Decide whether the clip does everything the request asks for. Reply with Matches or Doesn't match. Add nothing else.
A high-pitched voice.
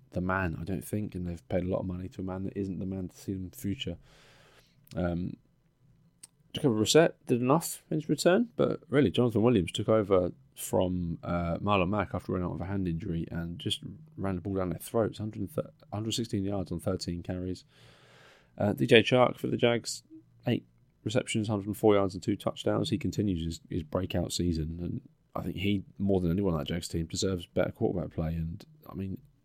Doesn't match